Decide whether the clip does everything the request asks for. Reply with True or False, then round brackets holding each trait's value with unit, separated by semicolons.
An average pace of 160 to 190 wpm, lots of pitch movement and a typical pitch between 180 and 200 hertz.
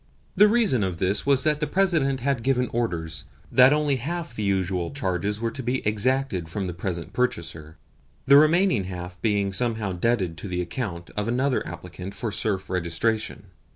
False (175 wpm; 6.6 semitones; 105 Hz)